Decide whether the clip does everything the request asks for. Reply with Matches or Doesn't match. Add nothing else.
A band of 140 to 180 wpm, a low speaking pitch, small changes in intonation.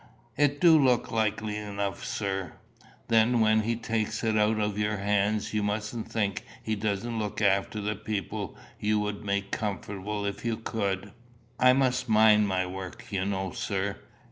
Matches